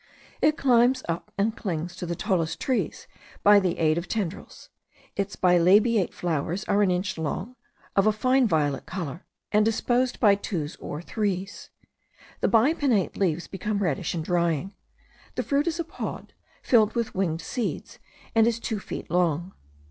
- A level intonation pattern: No, average, 4.7 semitones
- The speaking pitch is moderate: No, high, 195 Hz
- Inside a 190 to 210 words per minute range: No, average, 160 wpm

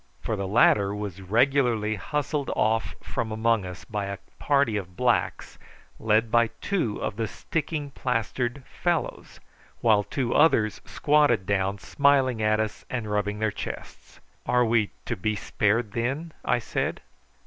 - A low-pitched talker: Yes, low, 115 Hz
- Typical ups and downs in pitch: Yes, average, 3.8 semitones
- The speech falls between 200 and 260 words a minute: No, average, 150 wpm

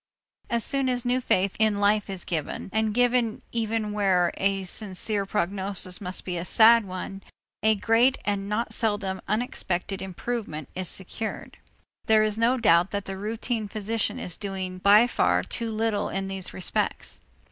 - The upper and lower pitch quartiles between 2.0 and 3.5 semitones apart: Yes, average, 2.9 semitones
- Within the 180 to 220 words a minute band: No, average, 160 wpm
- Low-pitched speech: No, high, 205 Hz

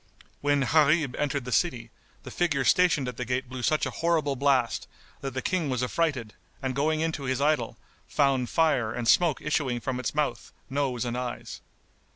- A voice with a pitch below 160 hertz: Yes, low, 135 Hz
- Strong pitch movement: No, average, 3.3 semitones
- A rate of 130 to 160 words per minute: No, average, 185 wpm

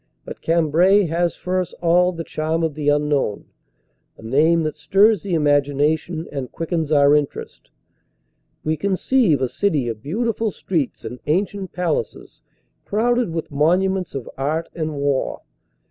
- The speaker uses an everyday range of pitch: Yes, average, 3.9 semitones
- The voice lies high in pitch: No, medium, 160 Hz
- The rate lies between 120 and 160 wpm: Yes, average, 145 wpm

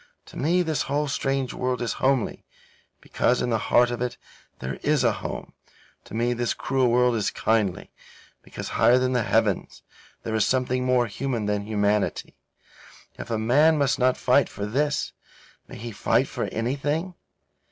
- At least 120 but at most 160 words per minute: No, average, 170 wpm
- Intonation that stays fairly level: No, average, 3.2 semitones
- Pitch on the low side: Yes, low, 125 Hz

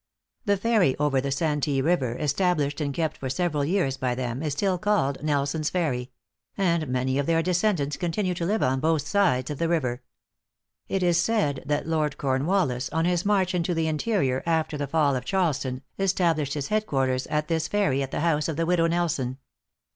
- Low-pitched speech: No, medium, 155 Hz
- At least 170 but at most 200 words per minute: Yes, average, 190 wpm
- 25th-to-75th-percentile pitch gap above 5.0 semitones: No, average, 4.4 semitones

